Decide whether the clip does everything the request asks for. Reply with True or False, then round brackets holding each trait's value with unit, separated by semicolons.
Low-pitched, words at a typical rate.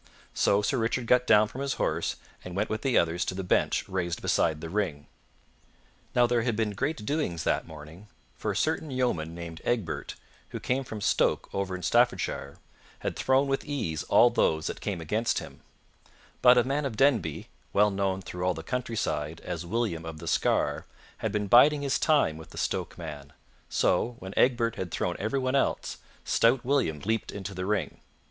True (105 Hz; 190 wpm)